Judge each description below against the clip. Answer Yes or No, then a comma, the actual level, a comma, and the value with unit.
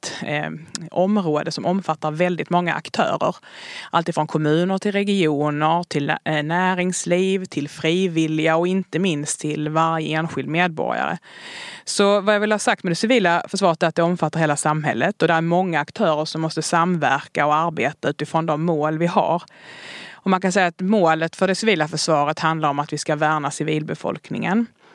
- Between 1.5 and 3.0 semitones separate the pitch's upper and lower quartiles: No, average, 3.4 semitones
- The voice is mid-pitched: Yes, medium, 165 Hz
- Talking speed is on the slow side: No, average, 165 wpm